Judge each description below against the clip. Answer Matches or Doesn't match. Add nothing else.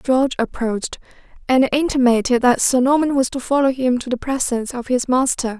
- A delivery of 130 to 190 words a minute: Matches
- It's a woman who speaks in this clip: Matches